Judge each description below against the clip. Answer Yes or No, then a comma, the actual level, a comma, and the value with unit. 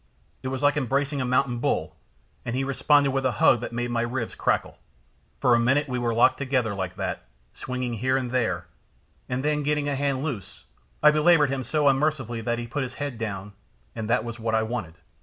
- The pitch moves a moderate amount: Yes, average, 3.0 semitones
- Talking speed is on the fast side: Yes, fast, 215 wpm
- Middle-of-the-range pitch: No, low, 125 Hz